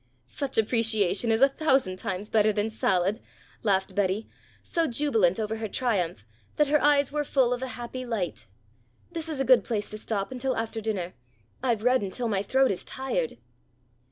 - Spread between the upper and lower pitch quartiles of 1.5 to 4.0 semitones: No, average, 4.5 semitones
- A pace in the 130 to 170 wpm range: No, average, 180 wpm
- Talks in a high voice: Yes, high, 225 Hz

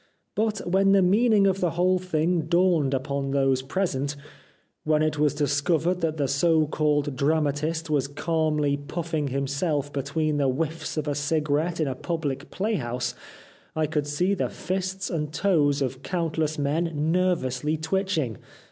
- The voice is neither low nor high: Yes, medium, 155 Hz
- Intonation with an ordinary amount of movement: Yes, average, 3.4 semitones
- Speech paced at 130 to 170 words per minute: Yes, average, 155 wpm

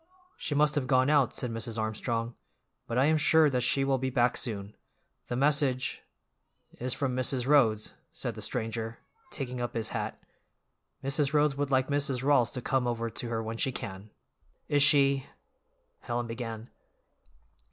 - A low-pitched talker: Yes, low, 125 Hz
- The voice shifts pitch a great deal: No, average, 3.1 semitones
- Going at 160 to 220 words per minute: Yes, average, 165 wpm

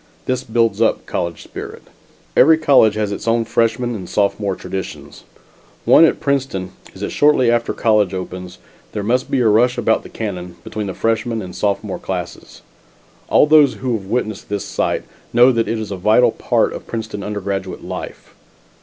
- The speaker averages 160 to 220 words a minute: Yes, average, 175 wpm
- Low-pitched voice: Yes, low, 110 Hz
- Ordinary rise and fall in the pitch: Yes, average, 3.3 semitones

